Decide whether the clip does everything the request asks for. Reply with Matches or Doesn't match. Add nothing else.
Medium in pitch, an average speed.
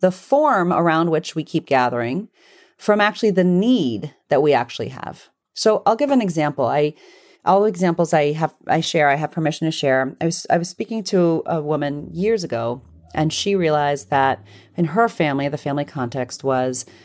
Matches